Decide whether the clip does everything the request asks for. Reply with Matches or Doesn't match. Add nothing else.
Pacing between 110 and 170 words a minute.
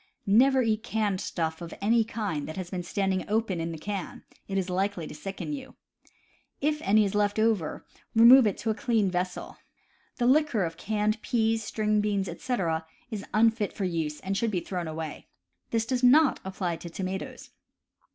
Doesn't match